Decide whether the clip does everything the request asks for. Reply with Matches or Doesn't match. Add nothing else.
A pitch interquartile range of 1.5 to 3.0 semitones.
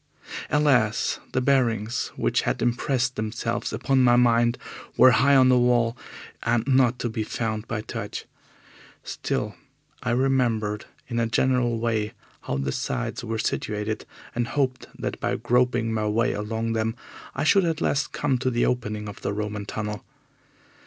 Matches